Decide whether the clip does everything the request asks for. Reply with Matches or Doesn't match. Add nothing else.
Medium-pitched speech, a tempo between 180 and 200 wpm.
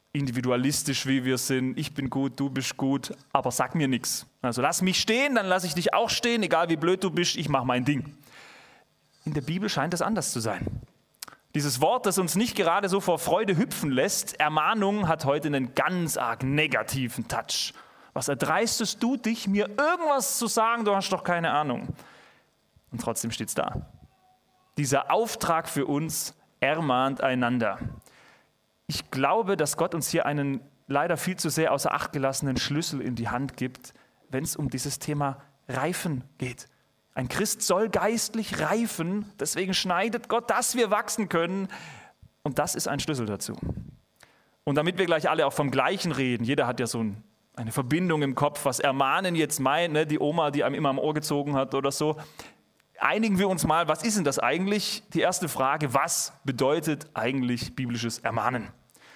Matches